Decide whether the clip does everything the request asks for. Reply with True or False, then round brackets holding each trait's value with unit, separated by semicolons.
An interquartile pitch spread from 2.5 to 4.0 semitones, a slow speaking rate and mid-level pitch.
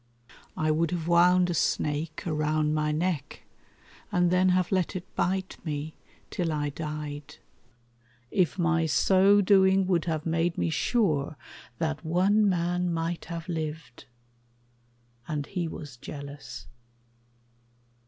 True (2.9 semitones; 125 wpm; 165 Hz)